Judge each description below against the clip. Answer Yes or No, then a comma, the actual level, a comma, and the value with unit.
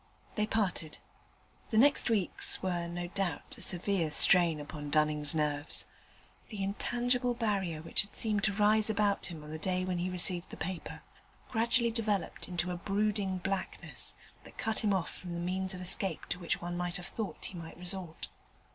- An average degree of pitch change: Yes, average, 3.4 semitones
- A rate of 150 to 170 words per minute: No, average, 180 wpm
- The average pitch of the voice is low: No, medium, 185 Hz